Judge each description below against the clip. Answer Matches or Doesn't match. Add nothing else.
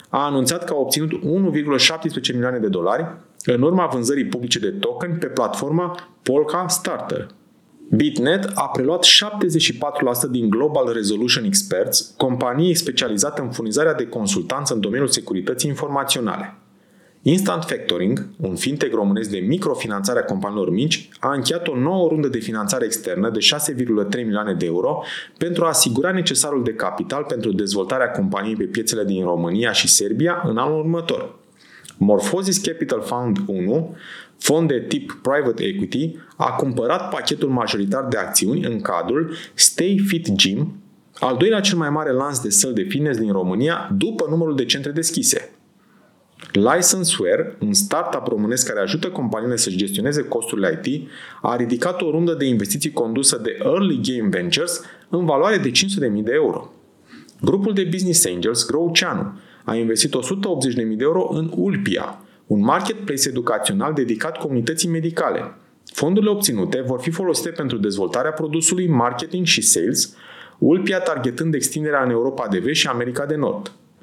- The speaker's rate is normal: Matches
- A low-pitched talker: Doesn't match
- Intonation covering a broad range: Matches